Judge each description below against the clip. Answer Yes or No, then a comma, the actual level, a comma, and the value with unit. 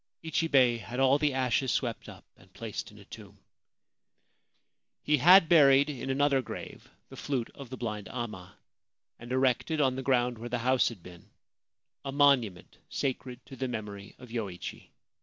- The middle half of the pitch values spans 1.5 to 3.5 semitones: Yes, average, 2.9 semitones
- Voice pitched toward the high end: No, low, 130 Hz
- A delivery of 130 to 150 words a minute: No, average, 165 wpm